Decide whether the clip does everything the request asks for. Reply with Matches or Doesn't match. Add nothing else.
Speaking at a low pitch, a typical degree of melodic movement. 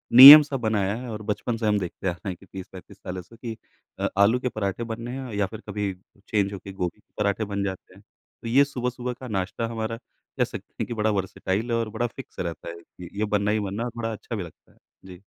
Matches